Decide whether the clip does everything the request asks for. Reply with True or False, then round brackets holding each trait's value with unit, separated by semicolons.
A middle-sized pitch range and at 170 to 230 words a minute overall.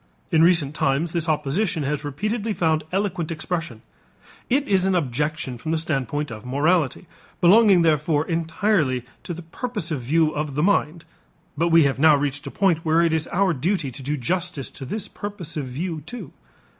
True (3.6 semitones; 175 wpm)